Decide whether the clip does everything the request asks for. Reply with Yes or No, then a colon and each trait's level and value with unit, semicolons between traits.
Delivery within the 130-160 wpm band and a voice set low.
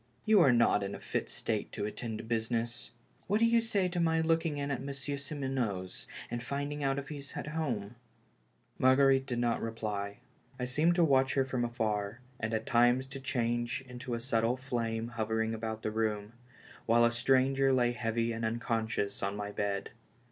No: average, 190 wpm; low, 120 Hz